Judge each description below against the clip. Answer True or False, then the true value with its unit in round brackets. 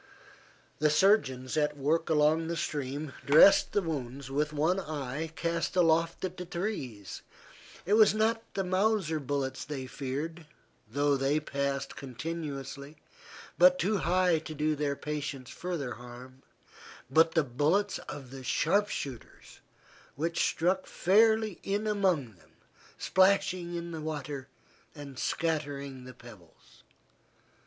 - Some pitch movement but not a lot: True (4.3 semitones)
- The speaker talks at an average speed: False (130 wpm)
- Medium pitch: True (155 Hz)